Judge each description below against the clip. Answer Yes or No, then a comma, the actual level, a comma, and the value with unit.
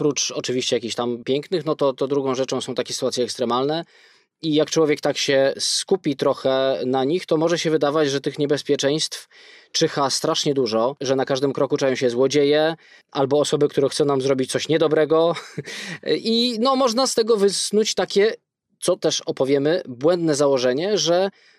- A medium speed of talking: No, fast, 170 wpm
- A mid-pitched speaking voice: Yes, medium, 145 Hz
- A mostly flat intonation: No, average, 3.7 semitones